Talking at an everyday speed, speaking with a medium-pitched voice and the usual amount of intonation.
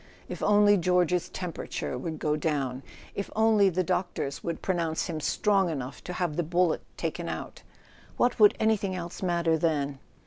Yes: average, 170 wpm; medium, 175 Hz; average, 3.5 semitones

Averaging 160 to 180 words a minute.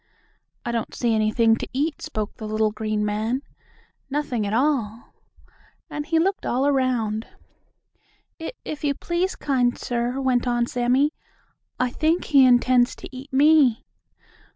No: average, 145 wpm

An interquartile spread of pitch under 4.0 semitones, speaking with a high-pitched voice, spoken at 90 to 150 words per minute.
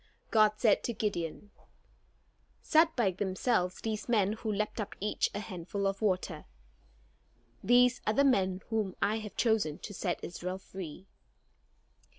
Yes: average, 2.9 semitones; high, 205 Hz; average, 145 wpm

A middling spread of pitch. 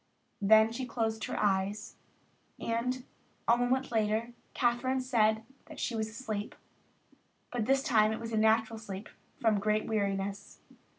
No: narrow, 2.1 semitones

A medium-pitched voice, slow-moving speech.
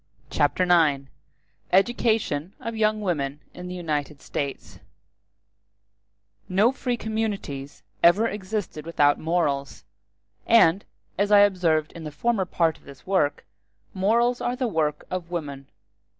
Yes: medium, 180 Hz; slow, 125 wpm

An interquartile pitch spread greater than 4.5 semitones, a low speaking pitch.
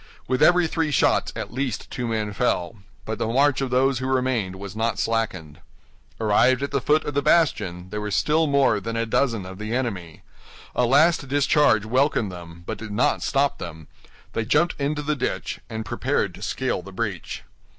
Yes: average, 5.2 semitones; low, 115 Hz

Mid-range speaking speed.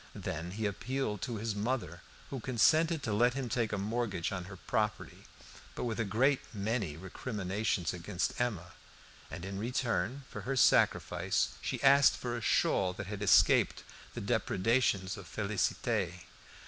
Yes: average, 155 wpm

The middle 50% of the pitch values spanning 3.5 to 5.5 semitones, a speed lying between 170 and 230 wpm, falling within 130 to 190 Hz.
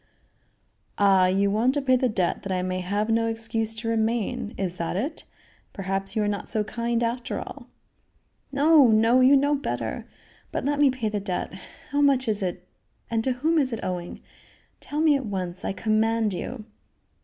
No: average, 4.7 semitones; average, 190 wpm; high, 225 Hz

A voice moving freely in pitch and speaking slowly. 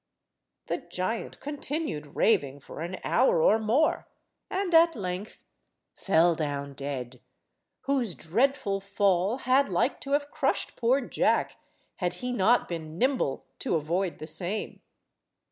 Yes: wide, 8.1 semitones; slow, 130 wpm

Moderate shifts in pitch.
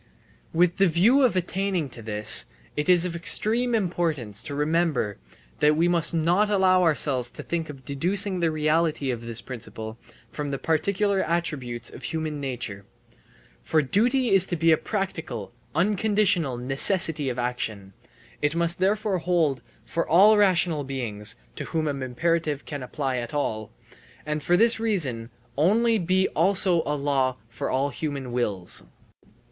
No: wide, 5.8 semitones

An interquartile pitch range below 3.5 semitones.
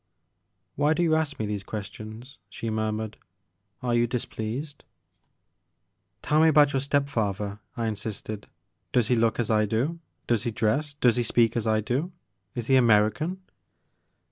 No: average, 4.7 semitones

